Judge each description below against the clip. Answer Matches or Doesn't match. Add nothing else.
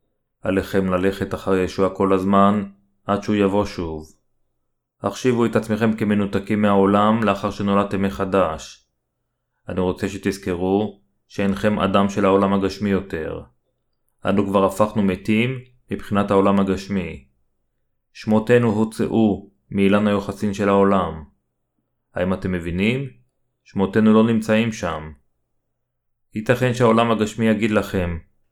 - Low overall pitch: Matches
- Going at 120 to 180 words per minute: Doesn't match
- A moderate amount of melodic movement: Doesn't match